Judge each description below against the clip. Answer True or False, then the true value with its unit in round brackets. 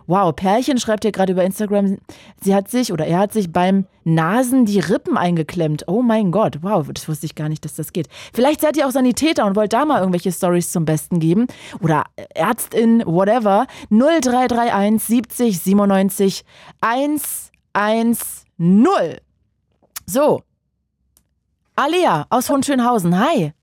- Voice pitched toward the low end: False (200 Hz)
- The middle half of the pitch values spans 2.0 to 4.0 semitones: False (5.4 semitones)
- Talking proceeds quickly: False (145 wpm)